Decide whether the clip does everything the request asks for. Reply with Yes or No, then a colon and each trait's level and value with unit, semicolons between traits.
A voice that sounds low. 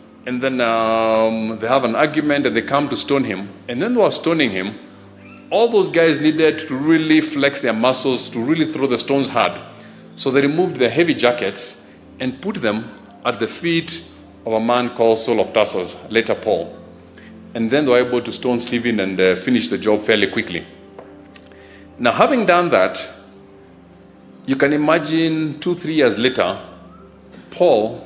Yes: low, 125 Hz